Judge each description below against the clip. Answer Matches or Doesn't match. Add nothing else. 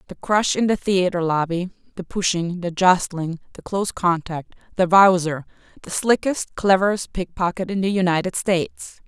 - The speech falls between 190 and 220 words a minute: Doesn't match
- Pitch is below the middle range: Doesn't match